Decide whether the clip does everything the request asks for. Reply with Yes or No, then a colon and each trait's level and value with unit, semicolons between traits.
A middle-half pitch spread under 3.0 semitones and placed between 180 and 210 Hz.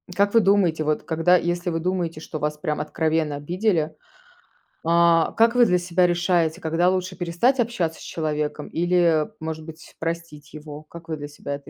No: narrow, 2.5 semitones; medium, 165 Hz